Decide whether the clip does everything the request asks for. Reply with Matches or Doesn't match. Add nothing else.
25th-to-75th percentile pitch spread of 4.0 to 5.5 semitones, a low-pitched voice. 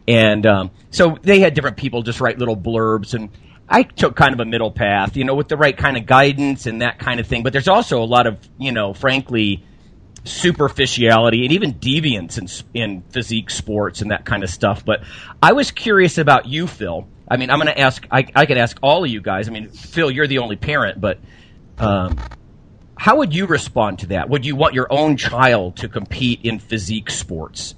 Matches